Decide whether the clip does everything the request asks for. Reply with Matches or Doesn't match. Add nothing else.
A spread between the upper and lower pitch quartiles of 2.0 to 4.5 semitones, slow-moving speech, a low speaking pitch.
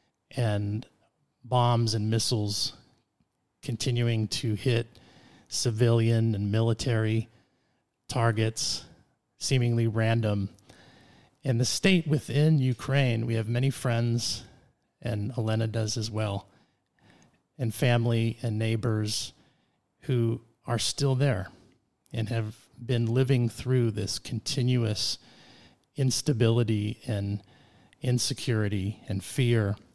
Matches